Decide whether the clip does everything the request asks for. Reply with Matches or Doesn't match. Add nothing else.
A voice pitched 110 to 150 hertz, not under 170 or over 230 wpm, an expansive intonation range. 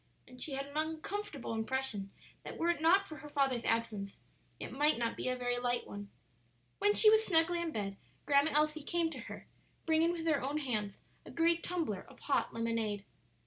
Doesn't match